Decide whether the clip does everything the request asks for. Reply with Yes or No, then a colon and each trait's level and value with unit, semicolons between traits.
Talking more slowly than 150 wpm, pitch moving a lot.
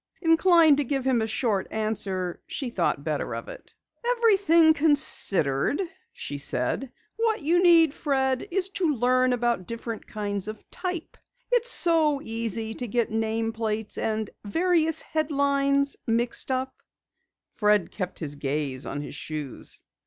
Yes: average, 140 wpm; wide, 7.0 semitones